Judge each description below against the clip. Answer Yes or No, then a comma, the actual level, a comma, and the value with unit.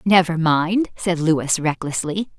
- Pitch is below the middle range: No, medium, 170 Hz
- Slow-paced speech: Yes, slow, 125 wpm